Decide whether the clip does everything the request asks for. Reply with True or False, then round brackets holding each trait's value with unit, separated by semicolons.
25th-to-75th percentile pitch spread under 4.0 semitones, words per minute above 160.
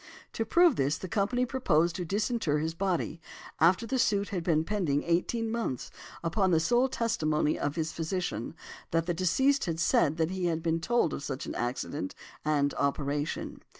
False (5.6 semitones; 180 wpm)